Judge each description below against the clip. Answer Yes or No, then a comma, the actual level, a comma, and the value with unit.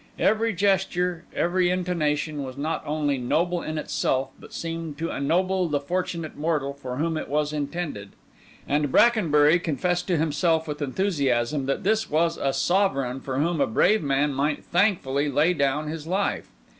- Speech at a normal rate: Yes, average, 160 wpm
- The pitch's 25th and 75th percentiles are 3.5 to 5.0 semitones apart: Yes, average, 3.8 semitones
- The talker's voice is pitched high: No, medium, 155 Hz